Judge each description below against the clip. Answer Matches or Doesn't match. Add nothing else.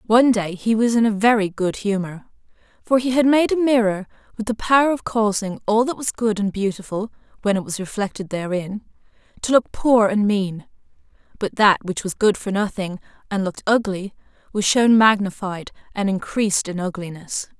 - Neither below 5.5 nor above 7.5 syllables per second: Doesn't match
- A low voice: Doesn't match